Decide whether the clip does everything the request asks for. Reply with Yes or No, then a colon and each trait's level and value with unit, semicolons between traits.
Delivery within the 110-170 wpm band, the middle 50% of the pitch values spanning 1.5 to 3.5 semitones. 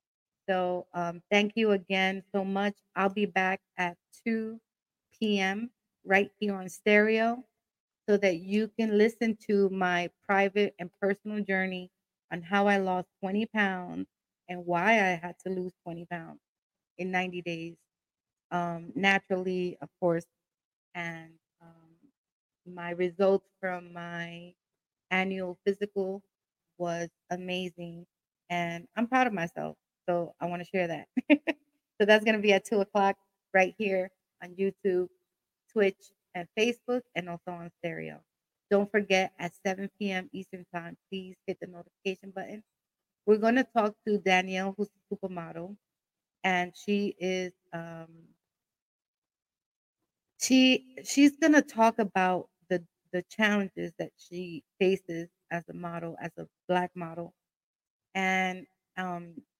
Yes: slow, 135 wpm; average, 2.7 semitones